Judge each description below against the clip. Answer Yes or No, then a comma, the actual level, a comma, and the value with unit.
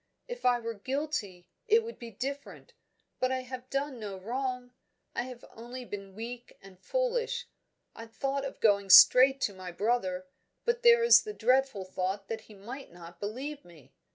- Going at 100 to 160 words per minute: No, average, 175 wpm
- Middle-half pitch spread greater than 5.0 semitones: Yes, wide, 5.5 semitones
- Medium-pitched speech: No, high, 245 Hz